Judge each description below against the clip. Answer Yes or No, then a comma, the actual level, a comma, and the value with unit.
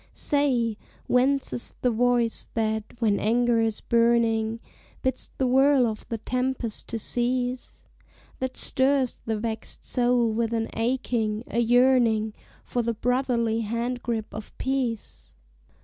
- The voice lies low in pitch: No, high, 235 Hz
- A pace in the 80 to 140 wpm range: Yes, slow, 135 wpm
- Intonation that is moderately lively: No, narrow, 2.0 semitones